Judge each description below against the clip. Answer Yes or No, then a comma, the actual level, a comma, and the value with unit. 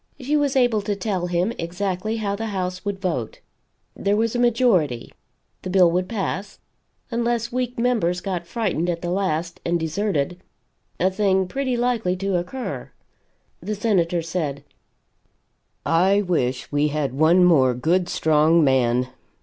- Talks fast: No, average, 150 wpm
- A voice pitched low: No, medium, 185 Hz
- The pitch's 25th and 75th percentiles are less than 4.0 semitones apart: No, average, 4.4 semitones